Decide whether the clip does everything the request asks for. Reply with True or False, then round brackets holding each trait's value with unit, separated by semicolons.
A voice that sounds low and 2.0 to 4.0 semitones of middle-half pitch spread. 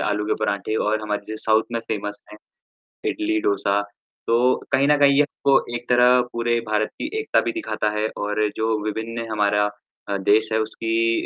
True (110 Hz; 2.6 semitones)